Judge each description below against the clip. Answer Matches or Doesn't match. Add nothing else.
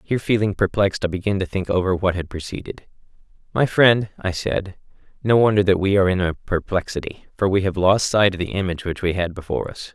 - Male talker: Matches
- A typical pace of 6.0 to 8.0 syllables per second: Matches